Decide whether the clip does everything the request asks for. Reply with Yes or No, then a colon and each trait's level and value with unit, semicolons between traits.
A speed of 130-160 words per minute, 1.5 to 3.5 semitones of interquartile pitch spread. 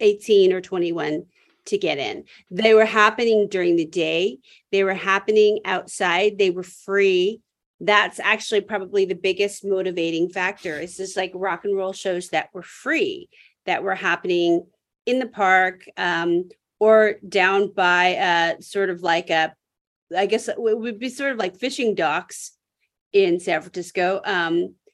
Yes: average, 155 wpm; average, 3.2 semitones